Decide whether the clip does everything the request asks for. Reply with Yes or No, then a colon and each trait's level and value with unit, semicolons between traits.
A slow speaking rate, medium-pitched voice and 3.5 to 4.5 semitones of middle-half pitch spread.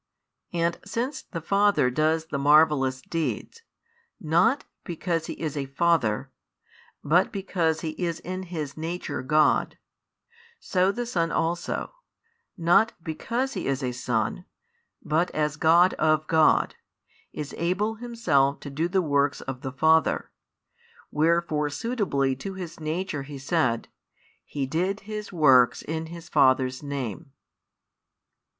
Yes: slow, 130 wpm; medium, 160 Hz; average, 4.2 semitones